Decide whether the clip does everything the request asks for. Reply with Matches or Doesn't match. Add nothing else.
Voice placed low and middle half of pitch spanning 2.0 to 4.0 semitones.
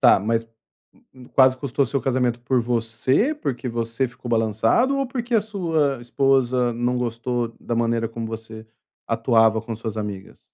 Matches